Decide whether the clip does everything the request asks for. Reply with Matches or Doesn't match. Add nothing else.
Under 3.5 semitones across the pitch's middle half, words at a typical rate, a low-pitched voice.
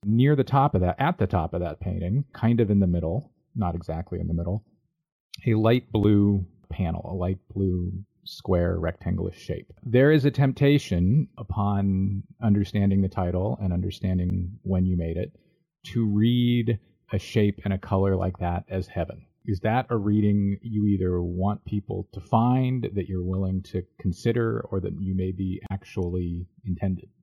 Doesn't match